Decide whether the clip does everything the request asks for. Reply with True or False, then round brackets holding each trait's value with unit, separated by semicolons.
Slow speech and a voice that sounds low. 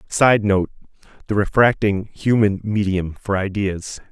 True (100 wpm; 100 Hz)